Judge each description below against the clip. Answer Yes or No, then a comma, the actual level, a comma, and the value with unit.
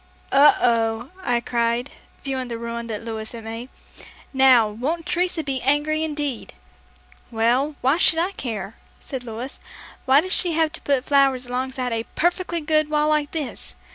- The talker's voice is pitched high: Yes, very high, 265 Hz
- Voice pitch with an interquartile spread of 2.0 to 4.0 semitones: No, average, 4.5 semitones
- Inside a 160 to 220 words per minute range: Yes, average, 170 wpm